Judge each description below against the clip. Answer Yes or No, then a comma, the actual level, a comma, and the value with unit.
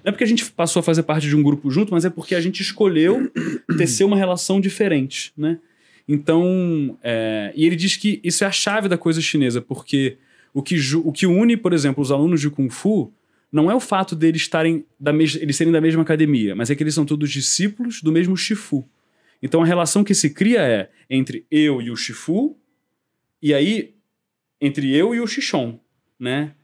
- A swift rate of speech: Yes, fast, 205 wpm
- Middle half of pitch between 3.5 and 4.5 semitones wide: No, average, 4.9 semitones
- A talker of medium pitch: Yes, medium, 160 Hz